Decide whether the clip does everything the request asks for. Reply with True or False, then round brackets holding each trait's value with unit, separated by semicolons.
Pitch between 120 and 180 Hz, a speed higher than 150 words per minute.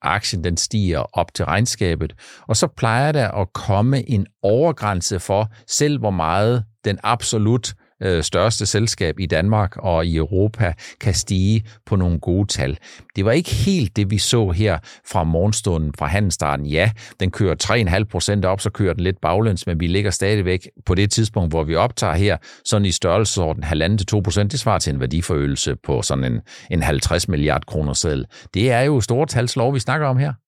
False (100 Hz; 190 wpm)